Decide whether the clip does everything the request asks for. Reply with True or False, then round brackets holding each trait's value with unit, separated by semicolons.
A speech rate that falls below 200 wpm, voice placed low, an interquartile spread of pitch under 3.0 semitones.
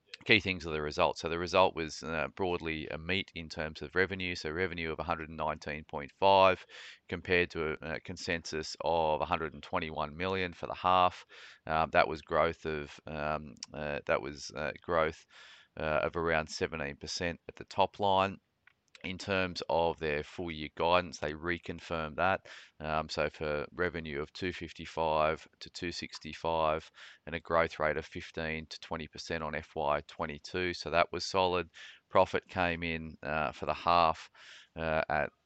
True (155 wpm; 80 Hz; 2.5 semitones)